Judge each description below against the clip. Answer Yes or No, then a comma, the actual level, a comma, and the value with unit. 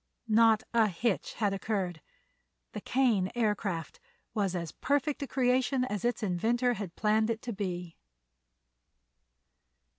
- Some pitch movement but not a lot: Yes, average, 4.2 semitones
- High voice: Yes, high, 215 Hz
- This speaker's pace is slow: Yes, slow, 125 wpm